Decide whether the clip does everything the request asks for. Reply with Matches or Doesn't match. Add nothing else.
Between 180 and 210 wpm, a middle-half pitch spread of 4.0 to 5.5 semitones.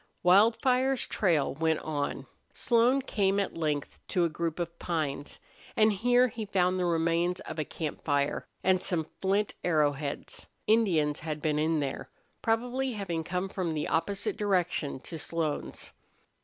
Doesn't match